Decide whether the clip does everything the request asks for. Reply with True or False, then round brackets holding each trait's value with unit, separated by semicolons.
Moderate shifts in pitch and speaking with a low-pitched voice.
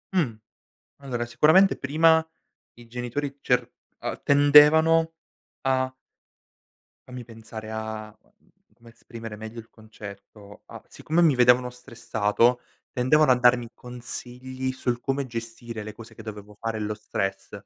True (3.0 semitones; 120 Hz)